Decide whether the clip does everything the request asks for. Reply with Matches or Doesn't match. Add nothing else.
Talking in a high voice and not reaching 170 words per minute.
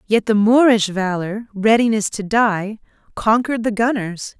Matches